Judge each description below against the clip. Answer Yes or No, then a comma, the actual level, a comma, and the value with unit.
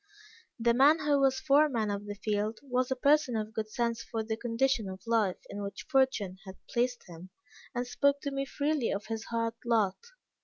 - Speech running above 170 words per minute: Yes, average, 195 wpm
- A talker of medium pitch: No, high, 230 Hz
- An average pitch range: Yes, average, 4.0 semitones